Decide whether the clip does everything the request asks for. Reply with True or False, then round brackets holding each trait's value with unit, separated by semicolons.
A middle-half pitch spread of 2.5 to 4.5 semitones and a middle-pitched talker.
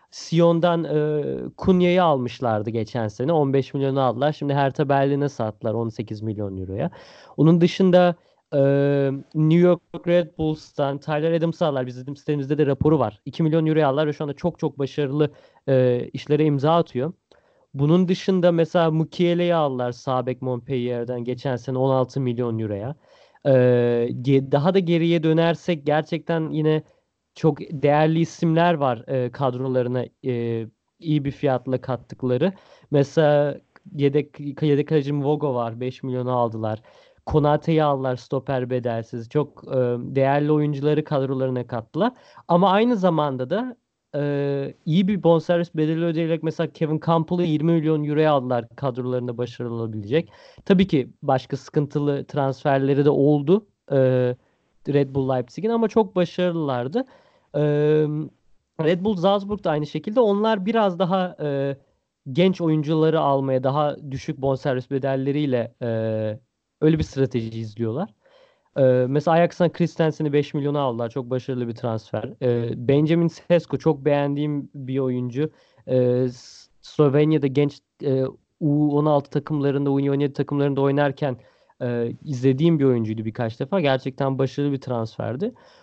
True (3.9 semitones; 145 Hz)